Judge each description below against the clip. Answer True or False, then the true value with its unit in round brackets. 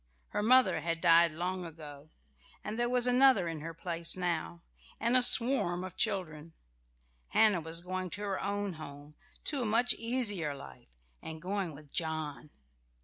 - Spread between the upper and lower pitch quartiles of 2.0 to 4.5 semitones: False (4.9 semitones)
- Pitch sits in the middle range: True (180 Hz)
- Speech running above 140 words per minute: True (160 wpm)